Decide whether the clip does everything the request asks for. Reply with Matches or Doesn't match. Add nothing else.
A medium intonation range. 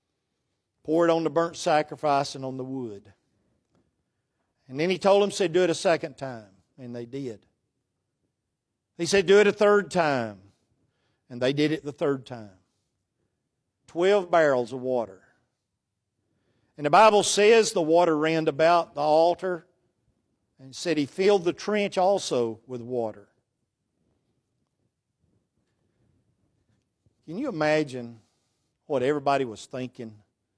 Doesn't match